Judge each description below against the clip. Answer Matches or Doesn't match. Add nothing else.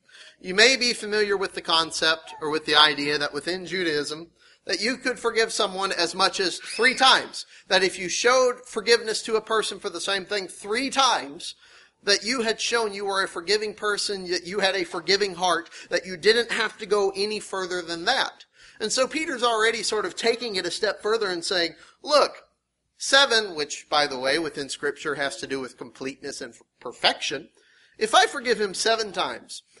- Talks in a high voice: Matches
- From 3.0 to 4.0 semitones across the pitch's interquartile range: Doesn't match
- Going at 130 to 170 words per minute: Doesn't match